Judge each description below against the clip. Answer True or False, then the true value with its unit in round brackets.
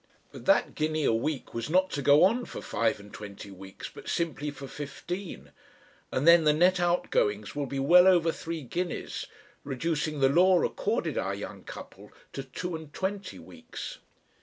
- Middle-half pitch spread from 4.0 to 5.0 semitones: True (4.7 semitones)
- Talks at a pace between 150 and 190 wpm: True (175 wpm)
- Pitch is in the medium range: True (155 Hz)